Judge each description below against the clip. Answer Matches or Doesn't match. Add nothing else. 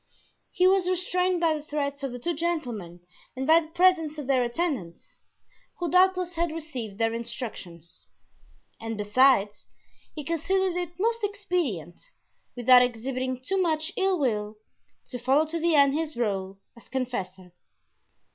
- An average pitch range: Doesn't match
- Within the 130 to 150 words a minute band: Matches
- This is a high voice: Matches